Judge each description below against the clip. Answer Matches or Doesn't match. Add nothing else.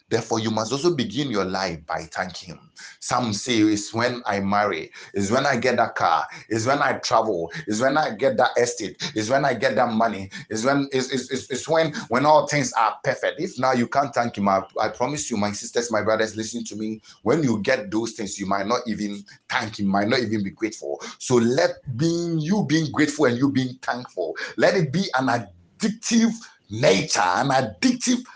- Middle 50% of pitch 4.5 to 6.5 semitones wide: Matches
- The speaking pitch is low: Matches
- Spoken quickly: Matches